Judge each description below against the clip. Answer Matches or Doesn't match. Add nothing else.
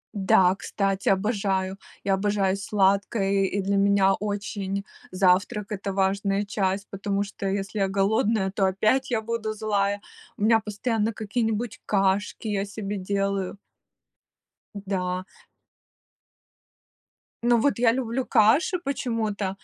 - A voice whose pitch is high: Matches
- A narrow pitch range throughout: Matches